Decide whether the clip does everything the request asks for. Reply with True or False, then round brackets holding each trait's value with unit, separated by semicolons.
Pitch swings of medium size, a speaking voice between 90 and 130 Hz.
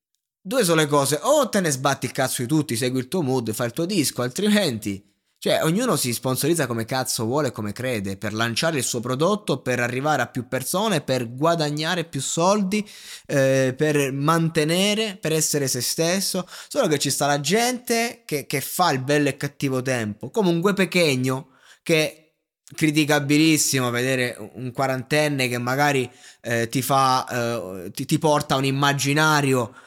False (4.0 semitones; 140 Hz)